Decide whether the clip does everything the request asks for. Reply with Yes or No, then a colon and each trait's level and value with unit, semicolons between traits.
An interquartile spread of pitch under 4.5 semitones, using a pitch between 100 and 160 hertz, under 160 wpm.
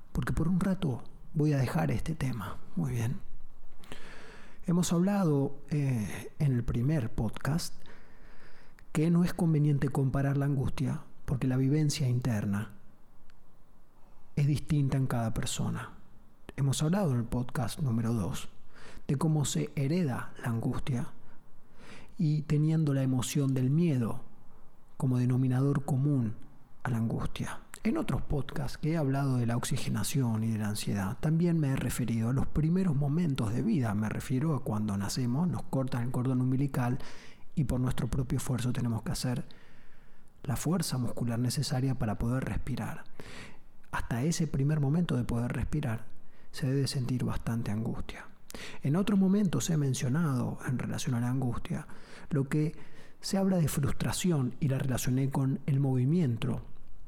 Yes: average, 3.7 semitones; low, 135 Hz; average, 150 wpm